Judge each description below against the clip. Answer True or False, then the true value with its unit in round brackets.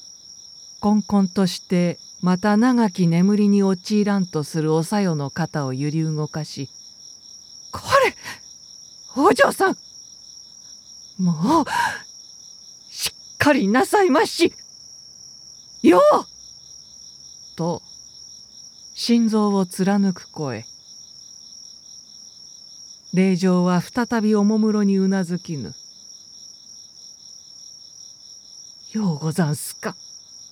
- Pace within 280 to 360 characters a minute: False (155 characters per minute)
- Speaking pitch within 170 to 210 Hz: True (190 Hz)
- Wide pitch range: False (4.0 semitones)